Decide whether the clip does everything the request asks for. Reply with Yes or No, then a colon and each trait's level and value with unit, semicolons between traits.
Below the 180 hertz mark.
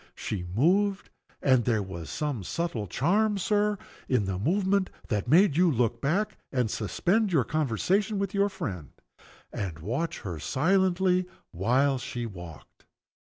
Yes: medium, 140 Hz